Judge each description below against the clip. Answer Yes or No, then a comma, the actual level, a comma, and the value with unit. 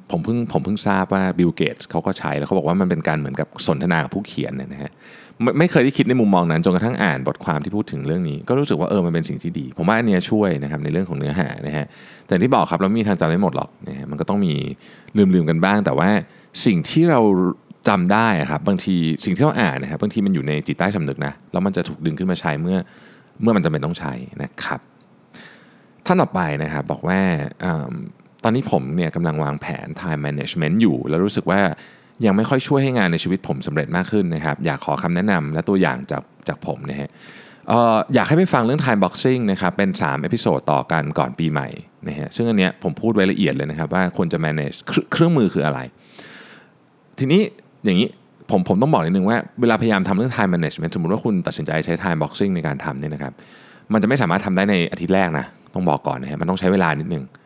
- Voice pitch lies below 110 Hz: Yes, very low, 90 Hz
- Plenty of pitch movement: Yes, wide, 5.9 semitones